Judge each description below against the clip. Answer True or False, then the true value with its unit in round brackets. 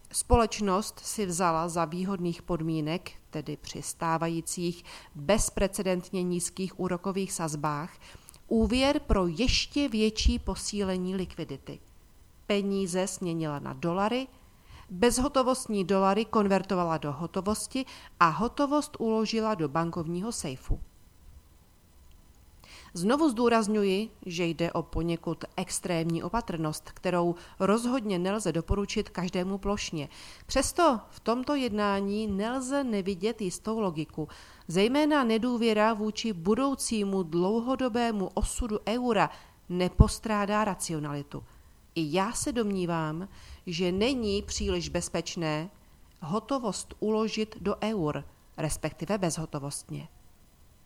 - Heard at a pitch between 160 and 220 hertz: True (190 Hz)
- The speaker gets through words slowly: True (95 wpm)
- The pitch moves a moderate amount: True (4.7 semitones)